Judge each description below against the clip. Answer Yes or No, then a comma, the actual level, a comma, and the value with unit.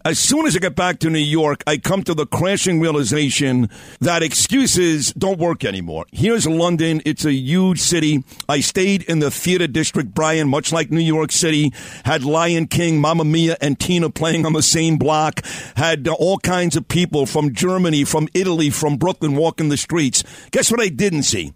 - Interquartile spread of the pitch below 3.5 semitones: Yes, average, 2.9 semitones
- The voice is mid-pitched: Yes, medium, 160 Hz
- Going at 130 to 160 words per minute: No, average, 190 wpm